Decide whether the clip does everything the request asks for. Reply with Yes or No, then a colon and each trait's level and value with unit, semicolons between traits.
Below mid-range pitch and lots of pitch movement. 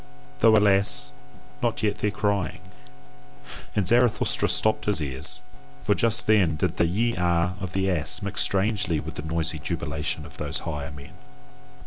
No: very low, 90 Hz; average, 4.6 semitones